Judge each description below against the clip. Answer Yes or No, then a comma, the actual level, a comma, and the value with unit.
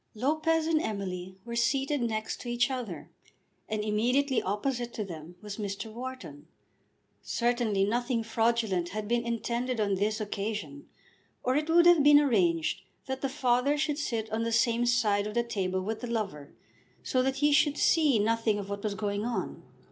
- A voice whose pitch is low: No, high, 230 Hz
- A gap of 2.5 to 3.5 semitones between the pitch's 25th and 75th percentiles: No, average, 3.9 semitones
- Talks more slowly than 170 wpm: No, average, 175 wpm